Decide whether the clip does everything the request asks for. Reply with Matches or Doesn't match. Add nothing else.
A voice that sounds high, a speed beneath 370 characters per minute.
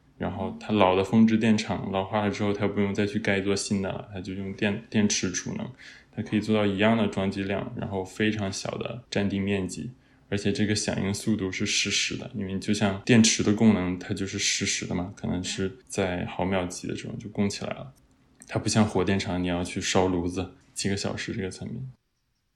Doesn't match